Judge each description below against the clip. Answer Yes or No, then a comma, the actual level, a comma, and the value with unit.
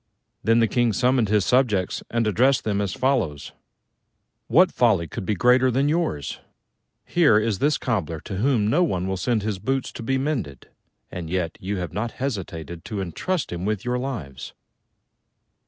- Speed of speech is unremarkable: Yes, average, 170 wpm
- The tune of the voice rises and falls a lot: Yes, wide, 5.7 semitones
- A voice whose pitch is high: No, low, 110 Hz